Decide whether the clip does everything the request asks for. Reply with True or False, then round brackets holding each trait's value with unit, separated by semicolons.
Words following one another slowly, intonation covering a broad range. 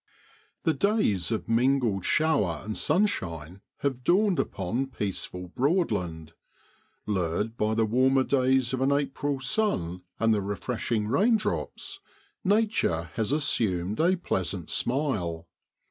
True (120 wpm; 7.0 semitones)